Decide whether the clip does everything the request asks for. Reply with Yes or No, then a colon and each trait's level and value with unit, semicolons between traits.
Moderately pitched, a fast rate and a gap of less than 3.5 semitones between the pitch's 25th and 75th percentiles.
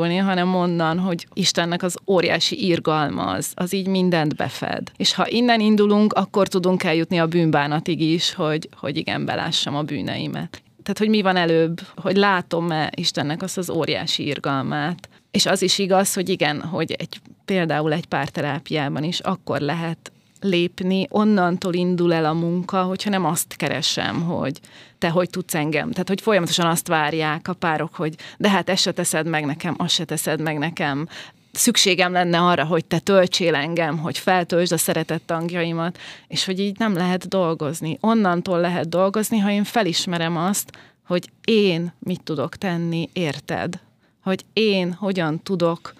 Yes: medium, 175 Hz; fast, 160 wpm; average, 2.8 semitones